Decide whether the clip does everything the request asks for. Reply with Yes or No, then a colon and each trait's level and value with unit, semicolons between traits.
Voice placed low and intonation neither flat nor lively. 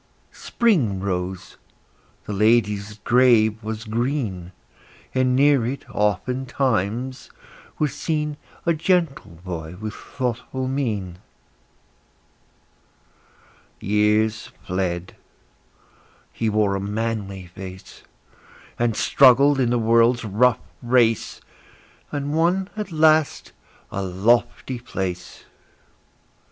Yes: low, 115 Hz; average, 4.9 semitones